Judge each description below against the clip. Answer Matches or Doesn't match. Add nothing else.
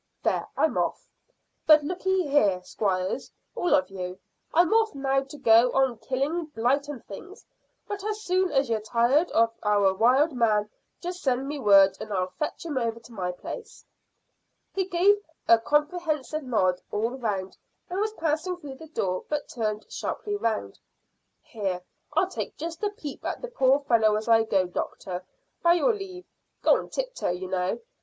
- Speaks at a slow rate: Doesn't match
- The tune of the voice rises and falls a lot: Matches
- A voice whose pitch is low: Doesn't match